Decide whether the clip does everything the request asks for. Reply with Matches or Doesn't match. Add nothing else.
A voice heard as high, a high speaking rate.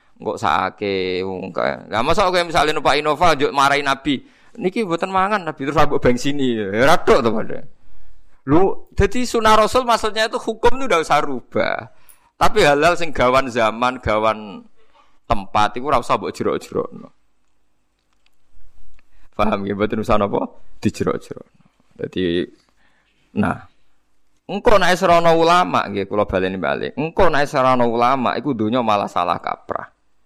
Doesn't match